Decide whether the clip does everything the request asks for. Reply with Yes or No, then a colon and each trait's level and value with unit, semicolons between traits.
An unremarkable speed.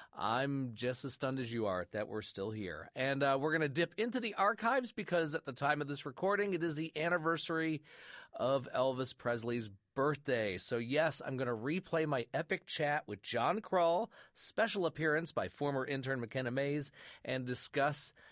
Yes: average, 185 wpm